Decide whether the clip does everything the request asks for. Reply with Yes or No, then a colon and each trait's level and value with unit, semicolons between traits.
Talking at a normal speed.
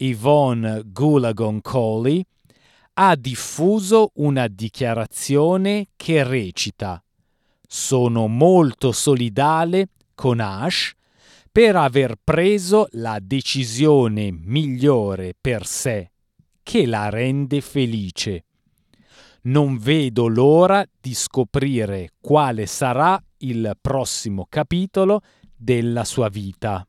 No: slow, 85 wpm